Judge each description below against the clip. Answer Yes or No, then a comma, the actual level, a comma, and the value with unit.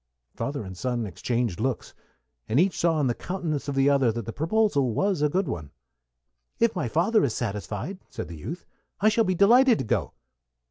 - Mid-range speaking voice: Yes, medium, 145 Hz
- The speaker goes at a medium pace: Yes, average, 195 wpm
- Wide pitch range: Yes, wide, 8.5 semitones